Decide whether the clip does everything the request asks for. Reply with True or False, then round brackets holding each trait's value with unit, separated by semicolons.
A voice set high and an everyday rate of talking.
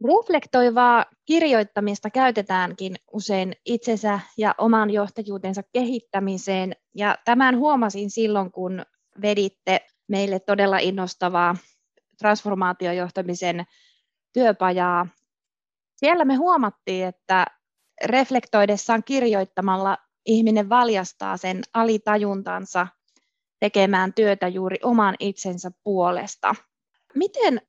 False (205 Hz; 80 wpm)